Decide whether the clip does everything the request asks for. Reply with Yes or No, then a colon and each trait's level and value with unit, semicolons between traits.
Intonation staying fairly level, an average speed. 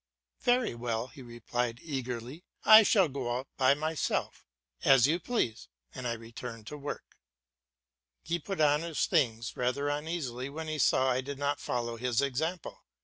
No: average, 4.4 semitones; average, 165 wpm